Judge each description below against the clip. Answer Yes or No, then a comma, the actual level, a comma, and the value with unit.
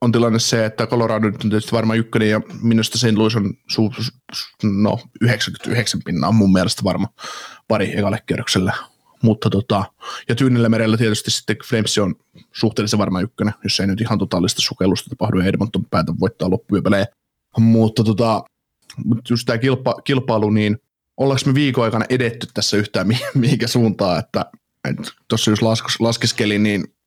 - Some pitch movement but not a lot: No, narrow, 2.0 semitones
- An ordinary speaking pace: No, fast, 165 wpm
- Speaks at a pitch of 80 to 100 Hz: No, low, 110 Hz